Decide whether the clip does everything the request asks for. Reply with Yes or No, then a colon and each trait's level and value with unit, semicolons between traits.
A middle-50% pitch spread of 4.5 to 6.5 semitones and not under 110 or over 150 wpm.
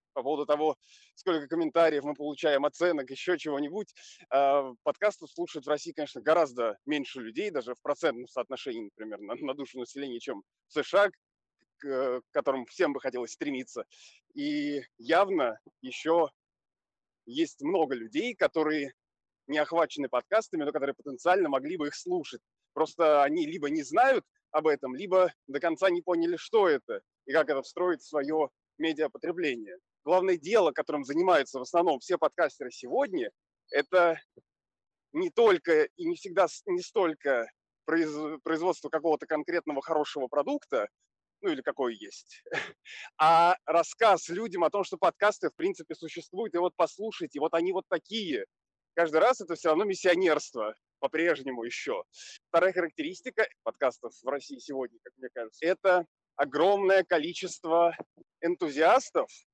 Yes: average, 5.2 semitones; average, 140 wpm